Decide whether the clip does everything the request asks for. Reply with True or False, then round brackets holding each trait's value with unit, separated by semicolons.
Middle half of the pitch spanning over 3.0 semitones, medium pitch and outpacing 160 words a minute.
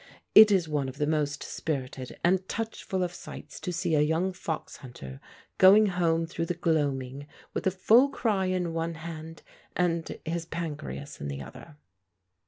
True (3.8 semitones; 165 Hz; 170 wpm)